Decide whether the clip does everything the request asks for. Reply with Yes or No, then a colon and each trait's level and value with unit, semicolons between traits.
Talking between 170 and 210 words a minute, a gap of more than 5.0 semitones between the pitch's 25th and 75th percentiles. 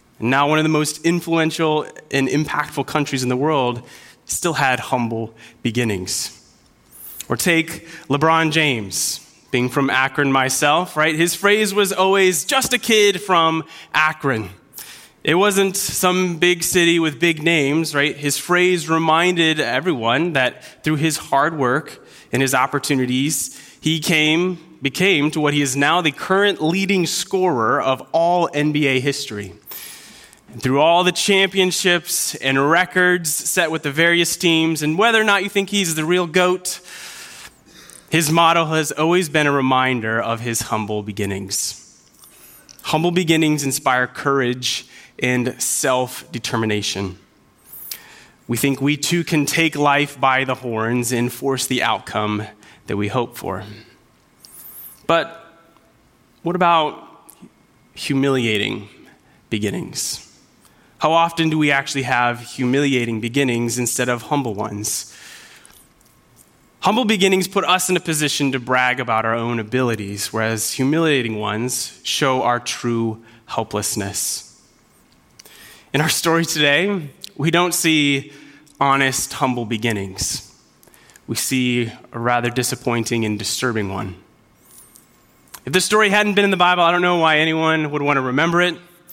No: slow, 135 wpm; wide, 5.4 semitones